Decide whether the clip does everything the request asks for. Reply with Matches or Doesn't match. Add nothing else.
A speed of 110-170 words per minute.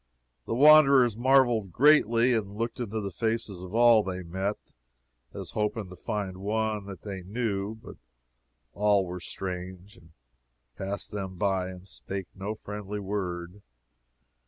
Matches